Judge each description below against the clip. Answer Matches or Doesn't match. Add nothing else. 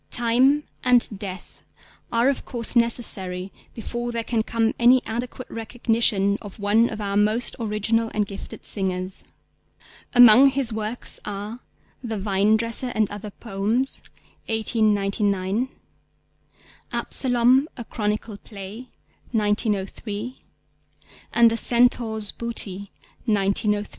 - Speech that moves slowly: Matches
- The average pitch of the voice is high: Matches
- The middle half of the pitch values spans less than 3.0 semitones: Matches